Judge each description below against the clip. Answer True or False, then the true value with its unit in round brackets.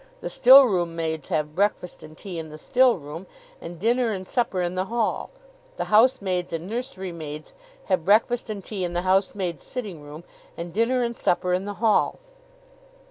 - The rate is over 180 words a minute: False (175 wpm)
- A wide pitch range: False (5.0 semitones)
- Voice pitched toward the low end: False (185 Hz)